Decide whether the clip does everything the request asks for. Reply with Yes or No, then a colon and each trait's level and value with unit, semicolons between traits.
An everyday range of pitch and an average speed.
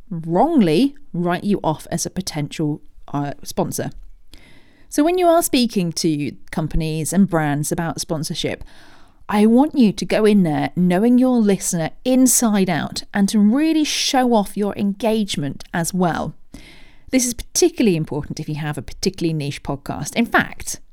No: wide, 6.6 semitones; average, 155 wpm